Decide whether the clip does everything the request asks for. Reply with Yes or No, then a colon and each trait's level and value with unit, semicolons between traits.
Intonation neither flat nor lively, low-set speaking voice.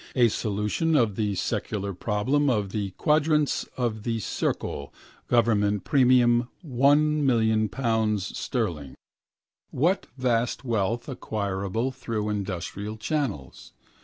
Yes: average, 3.8 semitones; low, 115 Hz